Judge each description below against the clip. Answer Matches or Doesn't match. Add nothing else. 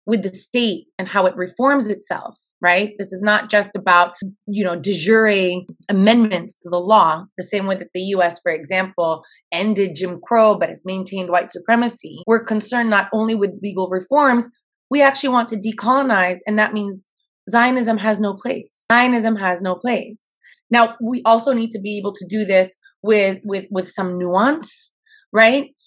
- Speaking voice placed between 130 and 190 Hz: Doesn't match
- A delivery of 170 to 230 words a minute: Matches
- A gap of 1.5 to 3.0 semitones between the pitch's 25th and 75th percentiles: Doesn't match